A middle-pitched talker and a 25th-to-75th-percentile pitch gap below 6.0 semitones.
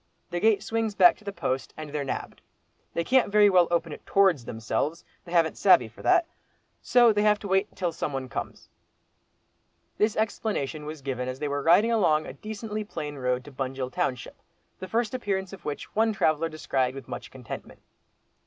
No: medium, 170 Hz; wide, 6.9 semitones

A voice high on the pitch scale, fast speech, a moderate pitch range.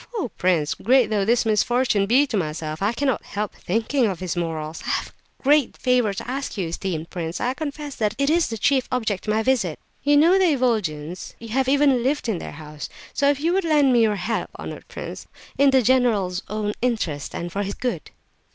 No: high, 225 Hz; fast, 220 wpm; wide, 6.2 semitones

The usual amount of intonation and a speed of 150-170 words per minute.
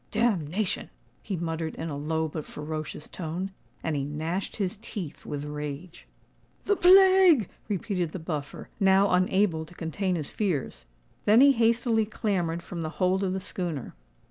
Yes: average, 4.5 semitones; average, 155 wpm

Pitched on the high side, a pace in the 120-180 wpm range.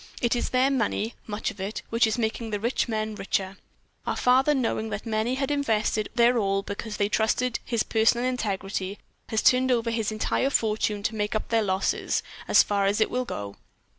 No: high, 220 Hz; average, 195 wpm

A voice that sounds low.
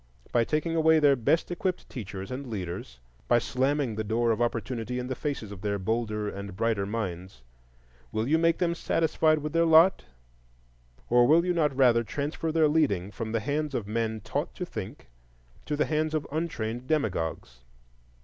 Yes: low, 125 Hz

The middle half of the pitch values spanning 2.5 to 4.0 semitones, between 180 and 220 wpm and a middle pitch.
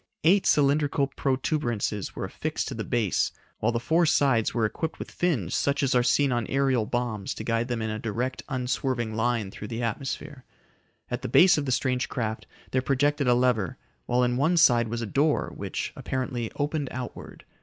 No: average, 3.4 semitones; average, 190 wpm; low, 125 Hz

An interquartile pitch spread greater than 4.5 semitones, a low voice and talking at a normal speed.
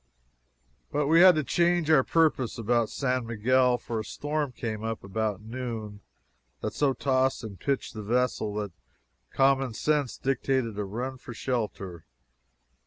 No: average, 3.8 semitones; low, 125 Hz; average, 150 wpm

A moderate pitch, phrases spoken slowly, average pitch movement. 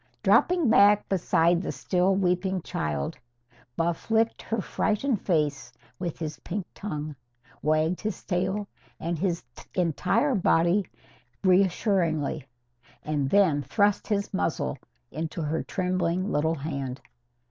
Yes: medium, 180 Hz; slow, 115 wpm; average, 4.1 semitones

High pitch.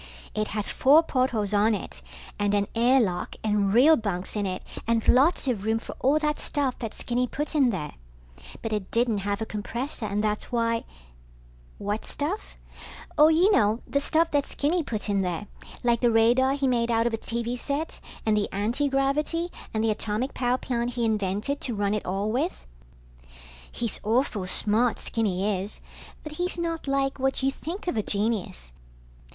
Yes: high, 235 Hz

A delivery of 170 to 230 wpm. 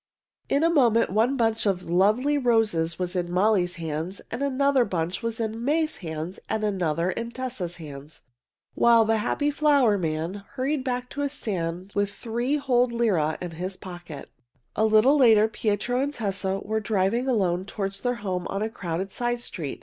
Yes: average, 180 wpm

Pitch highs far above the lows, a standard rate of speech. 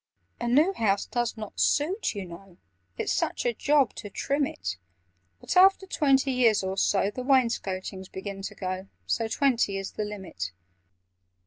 Yes: wide, 5.8 semitones; average, 160 wpm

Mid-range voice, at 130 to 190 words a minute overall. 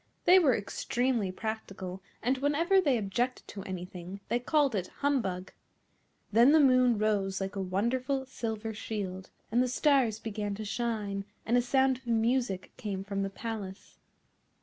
No: high, 225 Hz; average, 155 wpm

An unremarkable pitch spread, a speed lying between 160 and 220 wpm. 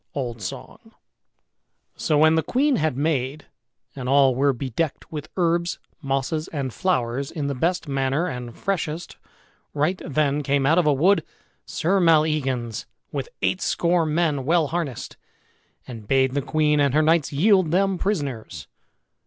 No: average, 3.8 semitones; average, 145 wpm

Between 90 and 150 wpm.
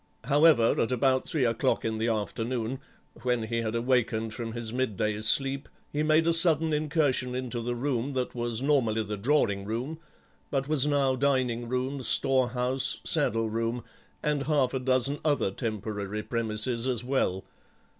No: average, 160 wpm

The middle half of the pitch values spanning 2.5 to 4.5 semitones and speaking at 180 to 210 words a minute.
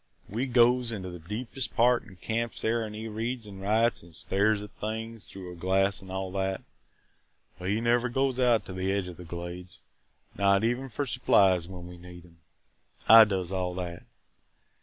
Yes: average, 4.0 semitones; average, 190 wpm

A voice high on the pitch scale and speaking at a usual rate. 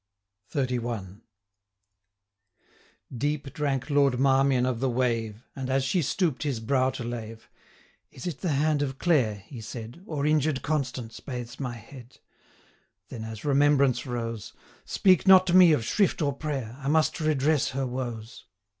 No: low, 135 Hz; average, 155 wpm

